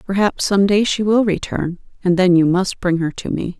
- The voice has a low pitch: No, high, 190 Hz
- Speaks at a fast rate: Yes, fast, 235 wpm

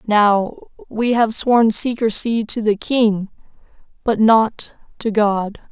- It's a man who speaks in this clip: No, female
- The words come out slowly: Yes, slow, 125 wpm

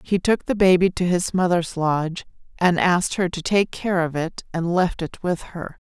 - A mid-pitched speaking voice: Yes, medium, 175 Hz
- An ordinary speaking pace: No, fast, 215 wpm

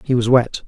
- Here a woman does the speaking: No, male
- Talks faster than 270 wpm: No, fast, 265 wpm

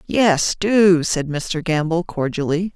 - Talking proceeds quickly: No, slow, 130 wpm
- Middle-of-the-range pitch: Yes, medium, 170 Hz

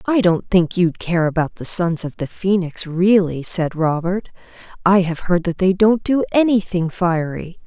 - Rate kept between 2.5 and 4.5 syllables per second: Yes, 4.3 syllables/s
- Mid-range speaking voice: Yes, medium, 180 Hz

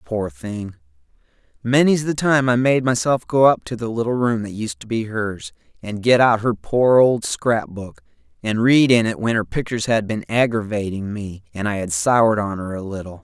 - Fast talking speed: Yes, fast, 210 wpm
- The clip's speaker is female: No, male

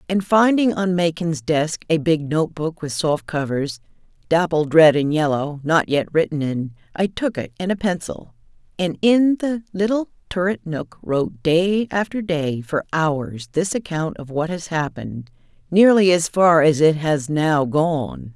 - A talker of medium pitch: Yes, medium, 165 Hz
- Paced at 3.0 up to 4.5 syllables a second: Yes, 4.2 syllables/s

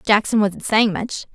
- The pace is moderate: Yes, average, 180 wpm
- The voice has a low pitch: No, high, 215 Hz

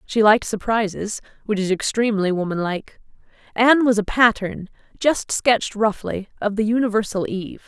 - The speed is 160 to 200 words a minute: No, slow, 135 wpm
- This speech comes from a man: No, female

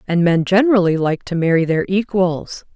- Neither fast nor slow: Yes, average, 175 wpm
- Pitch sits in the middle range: Yes, medium, 180 Hz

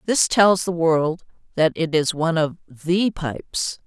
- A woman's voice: Yes, female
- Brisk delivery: No, average, 170 wpm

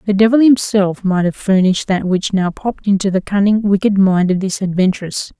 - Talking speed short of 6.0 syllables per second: Yes, 5.5 syllables/s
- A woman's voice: Yes, female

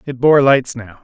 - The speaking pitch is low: Yes, low, 125 Hz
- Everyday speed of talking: No, fast, 230 wpm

